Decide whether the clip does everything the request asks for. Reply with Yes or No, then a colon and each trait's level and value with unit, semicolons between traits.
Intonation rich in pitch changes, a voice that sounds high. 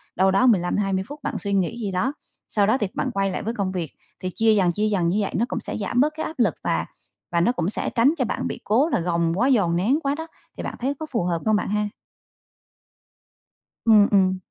No: average, 4.6 semitones; high, 205 Hz